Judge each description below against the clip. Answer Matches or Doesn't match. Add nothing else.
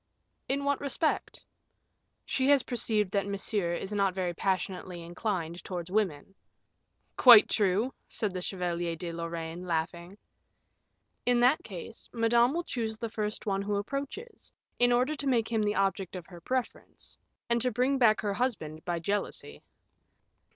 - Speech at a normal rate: Matches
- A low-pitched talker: Doesn't match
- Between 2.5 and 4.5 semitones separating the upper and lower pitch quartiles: Doesn't match